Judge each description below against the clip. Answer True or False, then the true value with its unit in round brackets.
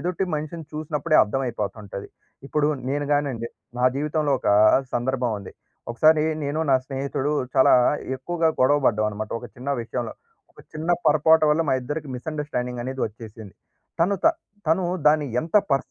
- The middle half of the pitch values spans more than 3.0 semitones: True (4.1 semitones)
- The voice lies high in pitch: False (140 Hz)